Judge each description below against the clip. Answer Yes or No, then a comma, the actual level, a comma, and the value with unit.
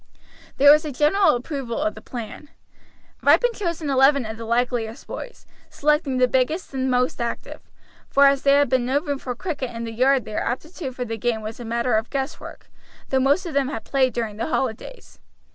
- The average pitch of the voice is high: Yes, very high, 260 Hz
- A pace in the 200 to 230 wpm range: Yes, fast, 205 wpm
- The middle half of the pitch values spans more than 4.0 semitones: No, average, 3.4 semitones